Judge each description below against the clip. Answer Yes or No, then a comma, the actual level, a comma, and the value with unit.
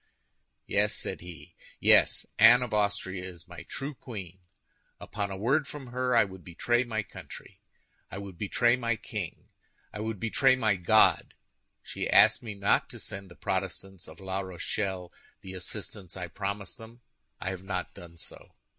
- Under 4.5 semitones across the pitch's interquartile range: Yes, average, 3.6 semitones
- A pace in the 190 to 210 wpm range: No, average, 165 wpm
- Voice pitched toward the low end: Yes, low, 100 Hz